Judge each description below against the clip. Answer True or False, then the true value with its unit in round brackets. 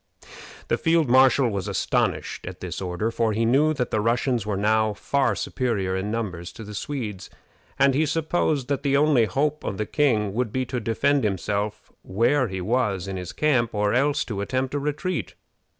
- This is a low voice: True (115 Hz)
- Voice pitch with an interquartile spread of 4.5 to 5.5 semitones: True (5.1 semitones)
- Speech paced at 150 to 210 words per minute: True (190 wpm)